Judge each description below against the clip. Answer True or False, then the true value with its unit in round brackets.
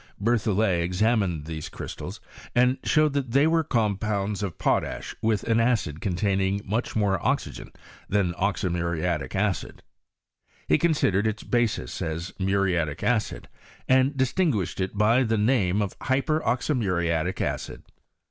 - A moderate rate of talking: False (130 wpm)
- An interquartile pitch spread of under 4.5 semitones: False (4.9 semitones)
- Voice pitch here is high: False (105 Hz)